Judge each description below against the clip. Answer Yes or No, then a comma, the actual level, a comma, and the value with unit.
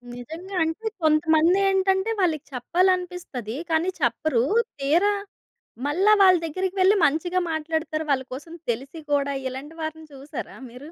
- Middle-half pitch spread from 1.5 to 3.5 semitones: No, average, 4.5 semitones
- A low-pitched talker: No, very high, 320 Hz